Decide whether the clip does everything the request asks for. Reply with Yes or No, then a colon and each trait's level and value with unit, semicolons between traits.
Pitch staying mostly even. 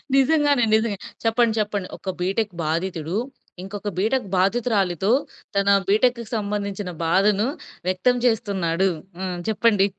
No: average, 3.1 semitones